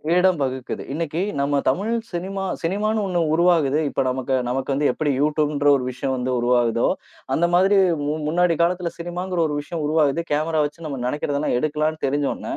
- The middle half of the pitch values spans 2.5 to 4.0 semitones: Yes, average, 3.7 semitones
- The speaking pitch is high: No, medium, 155 Hz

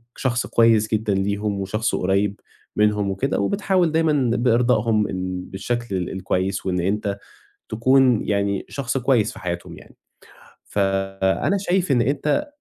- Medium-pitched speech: No, low, 110 Hz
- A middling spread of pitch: Yes, average, 4.7 semitones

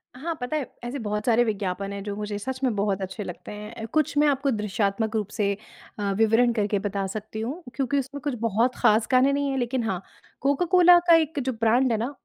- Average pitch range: Yes, average, 4.5 semitones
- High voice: Yes, high, 230 Hz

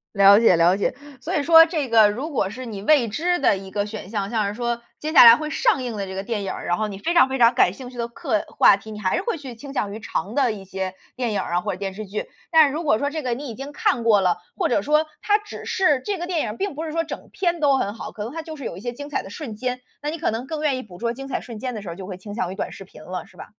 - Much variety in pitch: Yes, wide, 6.4 semitones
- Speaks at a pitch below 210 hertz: No, high, 235 Hz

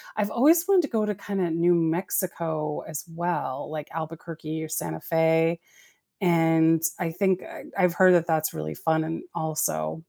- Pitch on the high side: No, medium, 165 Hz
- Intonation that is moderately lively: No, narrow, 2.2 semitones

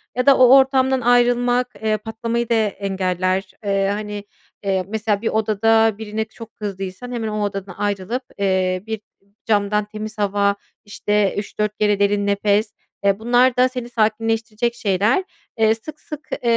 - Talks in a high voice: Yes, high, 215 Hz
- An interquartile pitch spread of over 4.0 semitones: No, average, 2.7 semitones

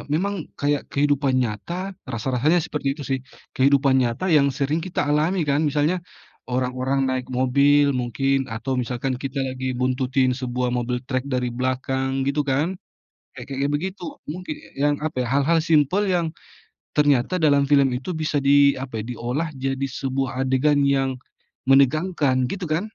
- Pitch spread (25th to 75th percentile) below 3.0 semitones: Yes, narrow, 2.6 semitones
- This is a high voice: No, low, 135 Hz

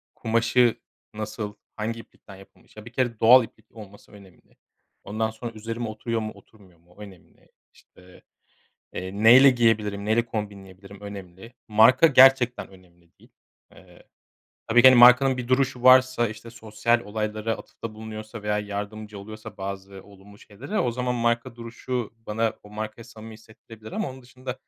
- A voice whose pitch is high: No, low, 110 Hz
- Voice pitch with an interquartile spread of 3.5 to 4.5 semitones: No, narrow, 2.4 semitones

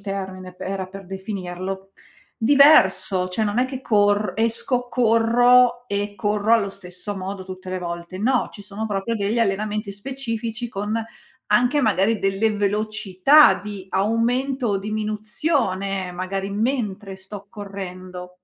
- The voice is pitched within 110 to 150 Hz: No, high, 205 Hz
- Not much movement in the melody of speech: No, average, 3.0 semitones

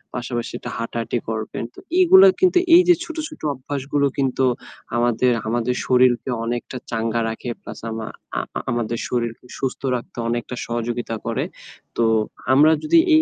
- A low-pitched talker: Yes, low, 120 Hz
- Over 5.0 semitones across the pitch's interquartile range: No, average, 2.9 semitones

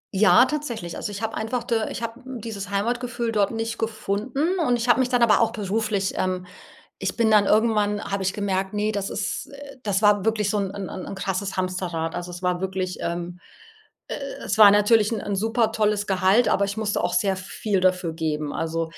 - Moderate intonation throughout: Yes, average, 3.1 semitones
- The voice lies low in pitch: No, high, 205 Hz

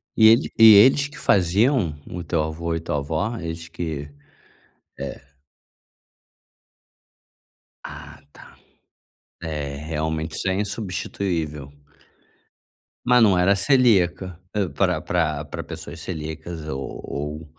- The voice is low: Yes, very low, 85 Hz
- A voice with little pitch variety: No, average, 4.4 semitones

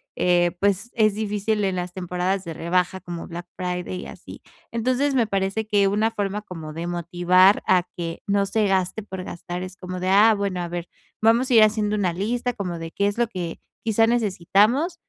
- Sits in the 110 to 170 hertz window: No, high, 195 Hz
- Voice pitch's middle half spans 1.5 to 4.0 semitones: Yes, average, 3.3 semitones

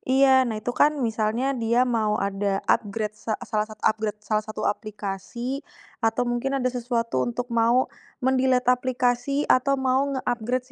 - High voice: Yes, high, 240 Hz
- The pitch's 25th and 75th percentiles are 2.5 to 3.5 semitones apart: Yes, average, 3.1 semitones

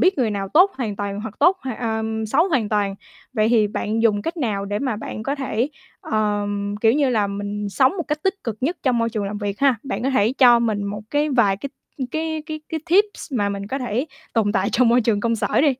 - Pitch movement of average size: Yes, average, 4.9 semitones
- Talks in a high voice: Yes, high, 225 Hz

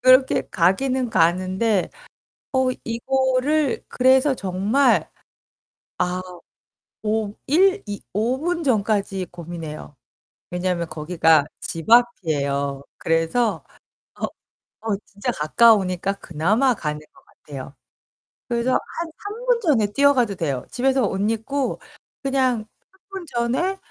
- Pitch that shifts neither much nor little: No, wide, 6.8 semitones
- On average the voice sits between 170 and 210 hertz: No, high, 220 Hz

